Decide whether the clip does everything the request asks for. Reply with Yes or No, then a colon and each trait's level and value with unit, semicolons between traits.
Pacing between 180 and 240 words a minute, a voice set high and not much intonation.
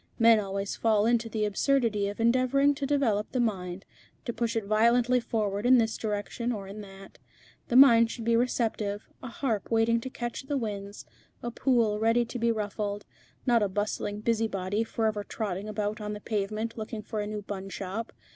Yes: average, 185 wpm; high, 220 Hz; narrow, 2.3 semitones